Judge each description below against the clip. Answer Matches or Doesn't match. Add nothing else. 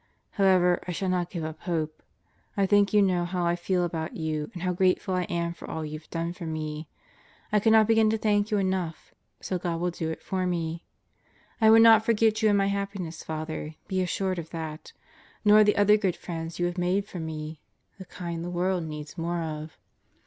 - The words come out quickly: Matches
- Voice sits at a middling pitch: Matches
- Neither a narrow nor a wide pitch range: Matches